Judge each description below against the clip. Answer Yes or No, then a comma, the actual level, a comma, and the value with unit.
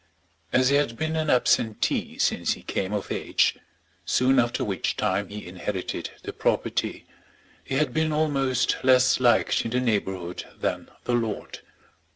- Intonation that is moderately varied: Yes, average, 4.5 semitones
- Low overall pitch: Yes, low, 125 Hz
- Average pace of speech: Yes, average, 155 wpm